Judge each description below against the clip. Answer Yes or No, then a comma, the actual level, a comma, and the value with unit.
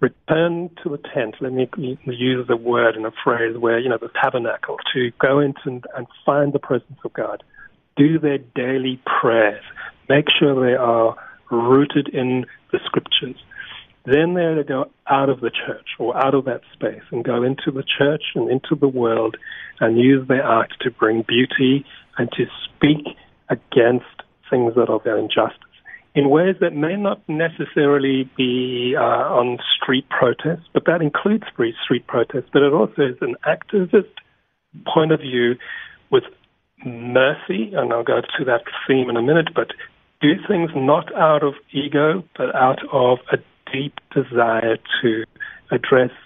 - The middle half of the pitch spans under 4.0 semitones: Yes, average, 3.6 semitones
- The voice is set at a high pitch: No, low, 135 Hz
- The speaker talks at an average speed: Yes, average, 165 wpm